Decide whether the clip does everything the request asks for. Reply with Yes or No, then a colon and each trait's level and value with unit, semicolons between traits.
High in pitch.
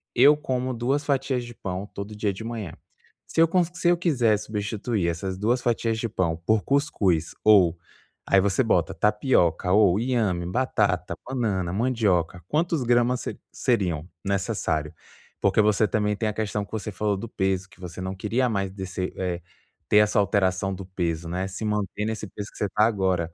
No: low, 105 Hz